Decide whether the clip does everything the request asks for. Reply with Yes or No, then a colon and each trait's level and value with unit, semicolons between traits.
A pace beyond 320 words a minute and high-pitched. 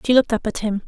Yes: fast, 340 wpm; high, 225 Hz